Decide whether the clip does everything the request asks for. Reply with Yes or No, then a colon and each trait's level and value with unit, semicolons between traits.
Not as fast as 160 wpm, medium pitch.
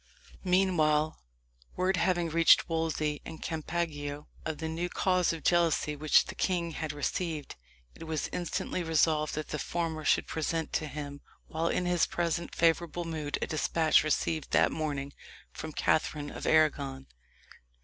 Yes: average, 150 wpm; medium, 160 Hz